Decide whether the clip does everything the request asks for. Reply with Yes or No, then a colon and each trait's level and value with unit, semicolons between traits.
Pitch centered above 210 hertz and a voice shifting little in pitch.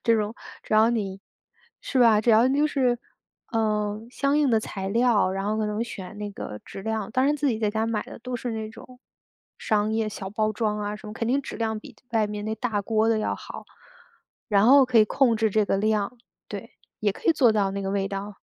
Yes: high, 220 Hz; narrow, 2.2 semitones